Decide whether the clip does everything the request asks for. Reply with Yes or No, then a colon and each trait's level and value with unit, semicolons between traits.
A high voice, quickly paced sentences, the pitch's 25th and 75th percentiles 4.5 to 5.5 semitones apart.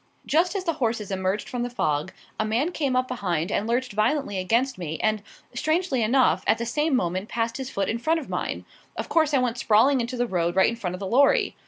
Yes: high, 235 Hz; fast, 235 wpm; average, 5.2 semitones